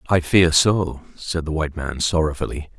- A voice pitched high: No, very low, 80 Hz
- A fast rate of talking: No, average, 170 wpm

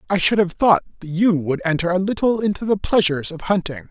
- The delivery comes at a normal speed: No, fast, 215 wpm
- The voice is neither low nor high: Yes, medium, 180 Hz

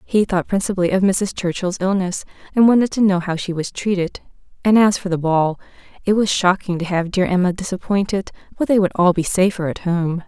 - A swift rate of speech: Yes, fast, 210 wpm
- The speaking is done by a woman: Yes, female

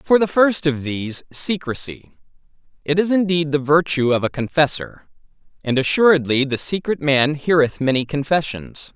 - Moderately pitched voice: Yes, medium, 150 Hz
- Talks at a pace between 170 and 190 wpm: No, average, 145 wpm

